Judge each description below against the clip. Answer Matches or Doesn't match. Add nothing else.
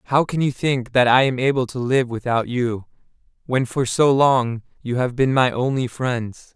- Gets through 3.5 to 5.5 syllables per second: Matches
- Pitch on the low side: Matches